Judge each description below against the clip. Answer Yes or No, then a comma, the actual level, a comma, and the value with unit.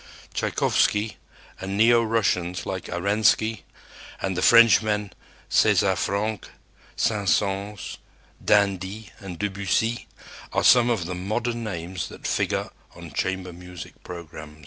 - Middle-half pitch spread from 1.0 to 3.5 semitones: Yes, average, 3.1 semitones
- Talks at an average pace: No, slow, 115 wpm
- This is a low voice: Yes, low, 100 Hz